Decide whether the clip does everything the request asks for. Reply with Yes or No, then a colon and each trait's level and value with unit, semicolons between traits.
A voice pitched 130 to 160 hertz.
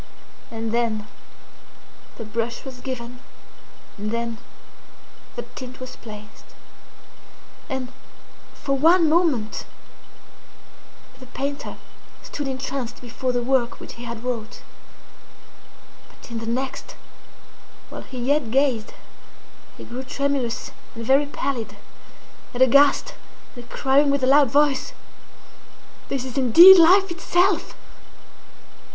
No: very high, 260 Hz